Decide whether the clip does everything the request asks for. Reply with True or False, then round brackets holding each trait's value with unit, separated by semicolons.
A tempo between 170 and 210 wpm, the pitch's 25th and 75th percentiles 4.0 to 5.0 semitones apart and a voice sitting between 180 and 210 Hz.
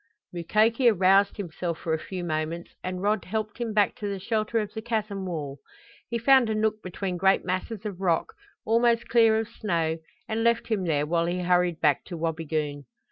True (190 wpm; 4.5 semitones; 190 Hz)